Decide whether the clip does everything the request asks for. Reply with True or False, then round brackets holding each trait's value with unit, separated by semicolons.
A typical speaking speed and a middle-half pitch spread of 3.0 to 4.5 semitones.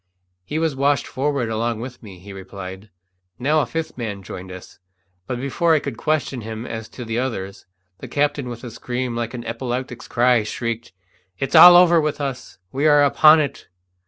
True (190 wpm; 4.2 semitones)